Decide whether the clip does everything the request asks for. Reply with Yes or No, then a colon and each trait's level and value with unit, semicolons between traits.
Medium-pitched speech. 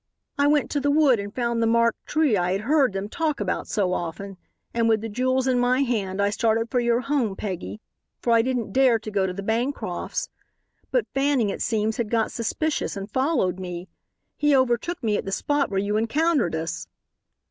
No: high, 230 Hz